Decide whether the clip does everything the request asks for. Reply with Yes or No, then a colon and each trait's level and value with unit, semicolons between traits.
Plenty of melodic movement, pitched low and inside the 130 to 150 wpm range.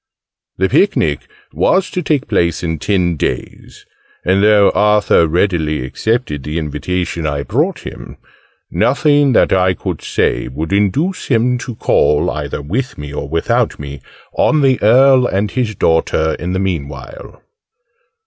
Yes: wide, 7.8 semitones; very low, 95 Hz; average, 145 wpm